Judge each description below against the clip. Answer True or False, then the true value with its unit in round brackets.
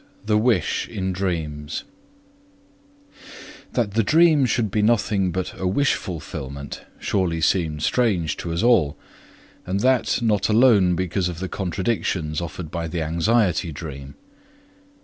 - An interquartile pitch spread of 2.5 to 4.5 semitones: False (5.0 semitones)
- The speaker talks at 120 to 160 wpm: True (145 wpm)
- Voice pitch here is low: True (95 Hz)